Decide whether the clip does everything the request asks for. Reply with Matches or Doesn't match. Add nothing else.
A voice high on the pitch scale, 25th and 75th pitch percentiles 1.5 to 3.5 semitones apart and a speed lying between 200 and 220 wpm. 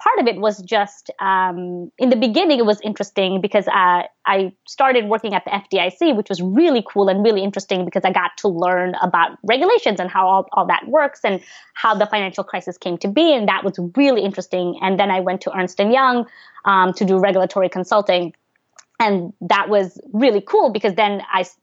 Matches